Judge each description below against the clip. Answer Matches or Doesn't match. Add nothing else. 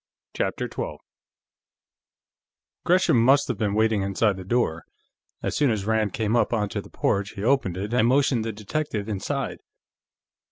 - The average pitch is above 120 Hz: Doesn't match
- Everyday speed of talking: Matches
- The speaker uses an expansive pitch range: Doesn't match